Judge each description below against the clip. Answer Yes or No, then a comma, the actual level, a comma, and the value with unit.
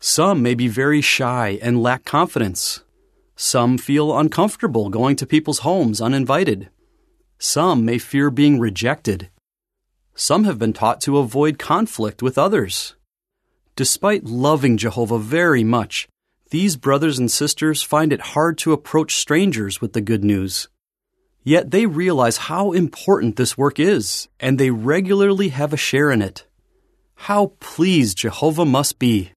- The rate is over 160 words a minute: No, average, 145 wpm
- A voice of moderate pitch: Yes, medium, 145 Hz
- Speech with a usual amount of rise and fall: No, wide, 6.1 semitones